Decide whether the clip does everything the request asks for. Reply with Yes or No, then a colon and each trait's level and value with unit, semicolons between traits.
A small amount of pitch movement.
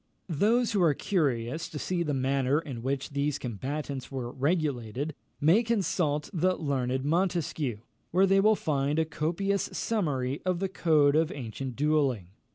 No: average, 4.8 semitones